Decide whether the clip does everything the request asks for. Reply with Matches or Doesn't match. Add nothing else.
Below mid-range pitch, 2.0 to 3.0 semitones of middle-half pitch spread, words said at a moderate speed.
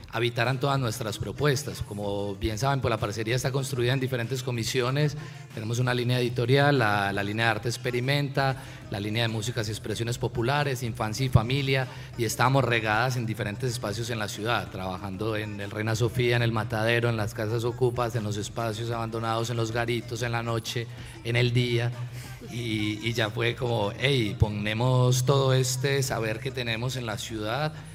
Matches